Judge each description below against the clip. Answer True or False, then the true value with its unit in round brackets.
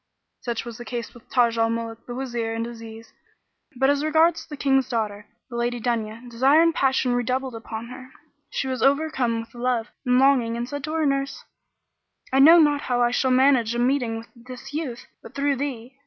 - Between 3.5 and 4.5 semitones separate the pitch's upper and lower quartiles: False (2.8 semitones)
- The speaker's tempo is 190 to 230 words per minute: True (205 wpm)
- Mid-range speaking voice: False (250 Hz)